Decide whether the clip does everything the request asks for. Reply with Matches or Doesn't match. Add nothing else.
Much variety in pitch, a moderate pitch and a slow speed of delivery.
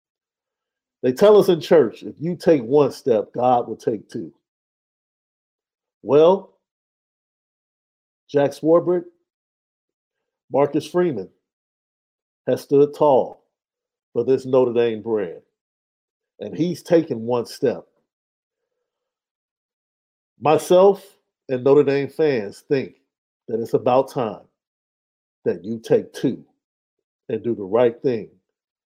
Matches